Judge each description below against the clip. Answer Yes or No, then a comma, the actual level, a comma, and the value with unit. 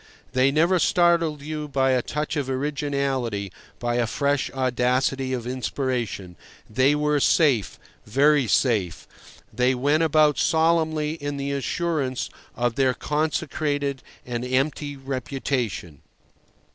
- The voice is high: No, low, 135 Hz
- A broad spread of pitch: No, average, 2.9 semitones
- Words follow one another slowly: Yes, slow, 120 wpm